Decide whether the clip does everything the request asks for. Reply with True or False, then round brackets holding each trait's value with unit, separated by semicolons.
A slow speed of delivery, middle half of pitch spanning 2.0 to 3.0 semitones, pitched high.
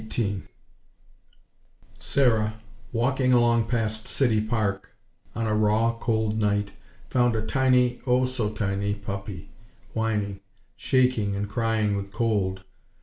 False (115 wpm; 2.6 semitones; 110 Hz)